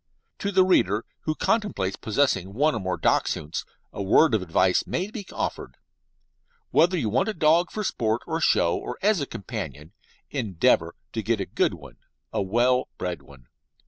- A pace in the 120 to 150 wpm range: No, average, 175 wpm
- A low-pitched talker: Yes, low, 115 Hz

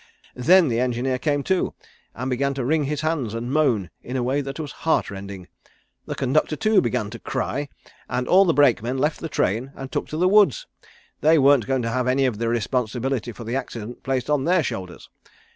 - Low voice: Yes, low, 130 Hz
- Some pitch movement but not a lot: Yes, average, 3.9 semitones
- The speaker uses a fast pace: Yes, fast, 210 wpm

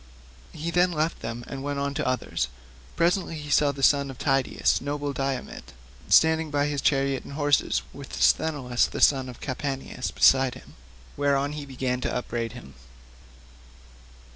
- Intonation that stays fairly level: Yes, narrow, 2.1 semitones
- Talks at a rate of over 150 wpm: Yes, average, 160 wpm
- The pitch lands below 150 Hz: Yes, medium, 140 Hz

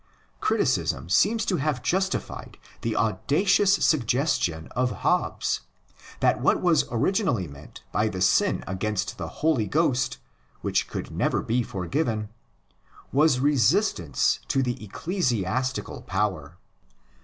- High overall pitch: No, low, 125 Hz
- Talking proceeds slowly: Yes, slow, 115 wpm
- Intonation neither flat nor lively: No, wide, 6.8 semitones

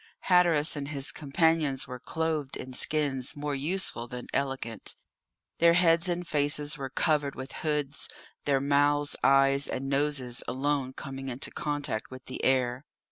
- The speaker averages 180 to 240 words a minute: No, average, 145 wpm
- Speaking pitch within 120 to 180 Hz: Yes, medium, 140 Hz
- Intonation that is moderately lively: No, narrow, 2.1 semitones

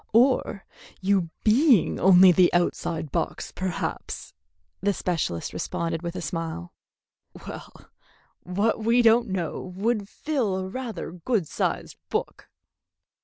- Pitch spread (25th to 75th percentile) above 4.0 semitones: Yes, average, 4.6 semitones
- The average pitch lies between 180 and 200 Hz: Yes, high, 190 Hz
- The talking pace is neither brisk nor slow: No, slow, 120 wpm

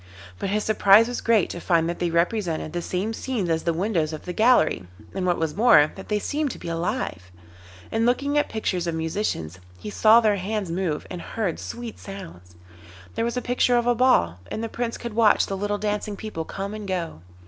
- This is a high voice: Yes, high, 200 Hz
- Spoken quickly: Yes, fast, 215 wpm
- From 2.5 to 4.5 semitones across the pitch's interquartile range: No, average, 5.0 semitones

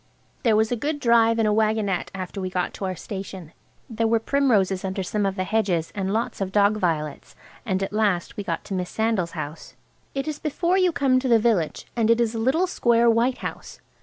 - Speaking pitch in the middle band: No, high, 215 Hz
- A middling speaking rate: No, fast, 220 wpm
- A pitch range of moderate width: Yes, average, 3.8 semitones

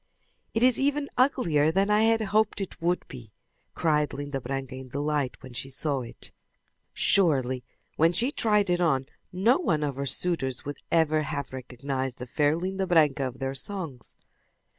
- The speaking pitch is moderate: Yes, medium, 150 Hz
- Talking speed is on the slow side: No, average, 170 wpm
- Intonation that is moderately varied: No, wide, 6.3 semitones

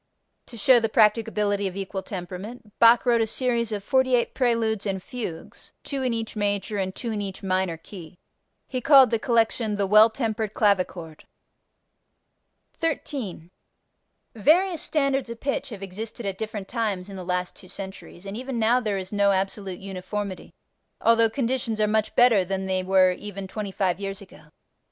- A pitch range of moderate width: Yes, average, 3.4 semitones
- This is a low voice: No, high, 210 Hz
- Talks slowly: No, average, 170 wpm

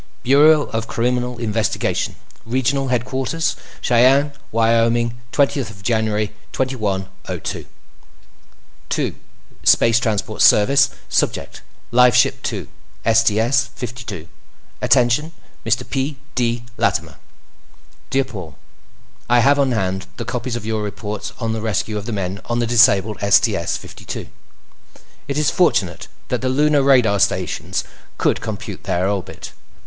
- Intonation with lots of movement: No, average, 3.5 semitones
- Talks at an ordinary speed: No, slow, 120 wpm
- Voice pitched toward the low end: Yes, low, 115 Hz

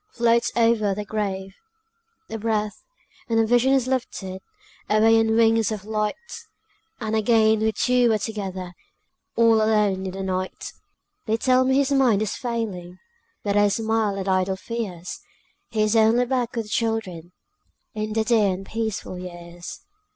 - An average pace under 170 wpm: Yes, average, 160 wpm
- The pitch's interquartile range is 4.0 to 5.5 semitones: No, average, 2.8 semitones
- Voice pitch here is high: Yes, high, 220 Hz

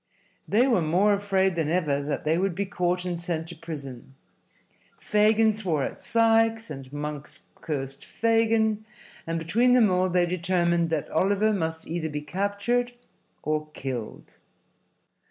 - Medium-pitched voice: Yes, medium, 180 Hz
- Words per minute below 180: Yes, average, 145 wpm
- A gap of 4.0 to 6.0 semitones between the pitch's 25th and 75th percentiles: Yes, average, 5.1 semitones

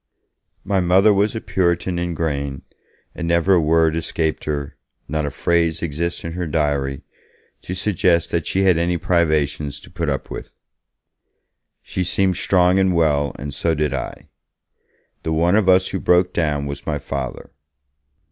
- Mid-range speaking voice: No, very low, 85 Hz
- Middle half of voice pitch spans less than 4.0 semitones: Yes, average, 3.3 semitones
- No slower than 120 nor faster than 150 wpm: No, average, 165 wpm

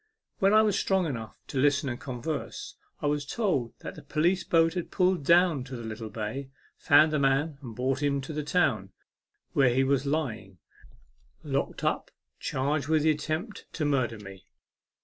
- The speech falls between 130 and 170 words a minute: No, average, 180 wpm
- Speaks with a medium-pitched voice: Yes, medium, 145 Hz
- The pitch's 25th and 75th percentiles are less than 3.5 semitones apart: No, average, 4.0 semitones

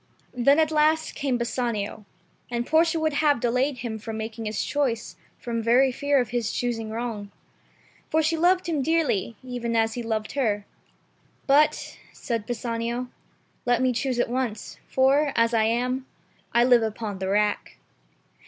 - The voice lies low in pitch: No, high, 245 Hz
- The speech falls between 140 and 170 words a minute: Yes, average, 160 wpm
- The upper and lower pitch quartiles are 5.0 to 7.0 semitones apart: No, average, 3.7 semitones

